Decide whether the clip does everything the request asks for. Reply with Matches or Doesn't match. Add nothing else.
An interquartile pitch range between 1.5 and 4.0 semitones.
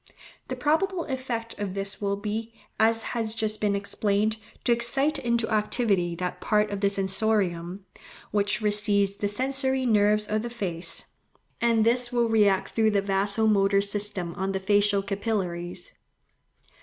Matches